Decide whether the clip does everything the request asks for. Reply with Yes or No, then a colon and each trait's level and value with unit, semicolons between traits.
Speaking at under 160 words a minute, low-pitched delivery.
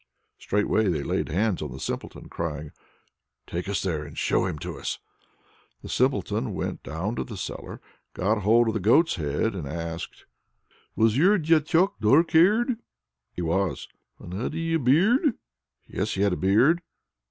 No: average, 165 wpm; low, 105 Hz